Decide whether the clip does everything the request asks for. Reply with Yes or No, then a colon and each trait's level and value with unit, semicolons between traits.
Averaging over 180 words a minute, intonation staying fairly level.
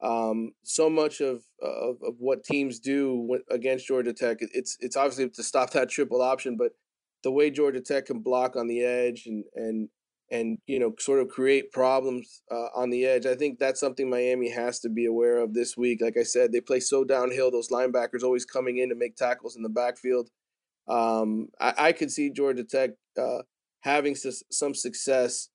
Yes: average, 200 wpm; narrow, 2.3 semitones